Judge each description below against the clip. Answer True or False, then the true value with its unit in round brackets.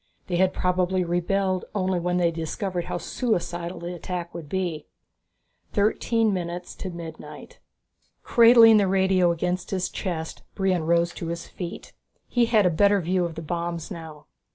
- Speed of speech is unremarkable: True (160 wpm)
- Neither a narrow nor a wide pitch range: False (2.0 semitones)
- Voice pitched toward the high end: False (180 Hz)